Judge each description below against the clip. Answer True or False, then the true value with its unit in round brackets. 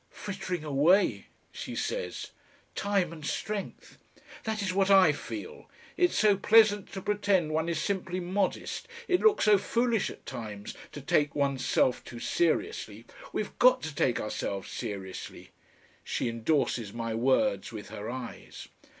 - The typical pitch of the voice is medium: True (175 Hz)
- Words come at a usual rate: True (145 wpm)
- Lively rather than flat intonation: True (8.2 semitones)